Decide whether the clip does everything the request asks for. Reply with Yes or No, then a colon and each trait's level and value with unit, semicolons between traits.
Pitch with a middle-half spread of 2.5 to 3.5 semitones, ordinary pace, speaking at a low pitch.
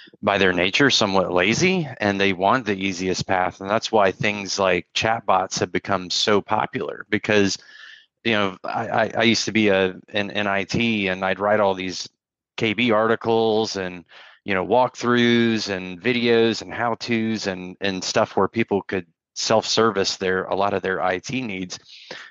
Yes: average, 3.2 semitones; average, 170 wpm; low, 100 Hz